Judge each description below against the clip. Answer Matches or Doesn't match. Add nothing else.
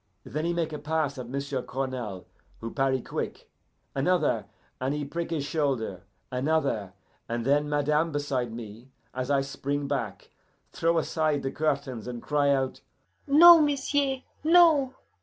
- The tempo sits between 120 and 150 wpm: Matches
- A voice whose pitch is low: Doesn't match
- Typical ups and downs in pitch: Matches